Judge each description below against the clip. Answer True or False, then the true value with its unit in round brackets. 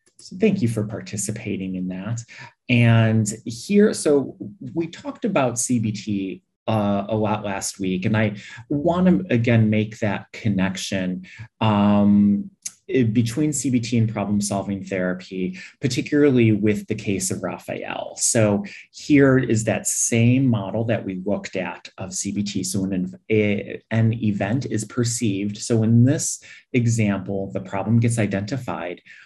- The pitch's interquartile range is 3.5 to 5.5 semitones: False (3.1 semitones)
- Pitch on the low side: True (110 Hz)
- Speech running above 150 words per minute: False (135 wpm)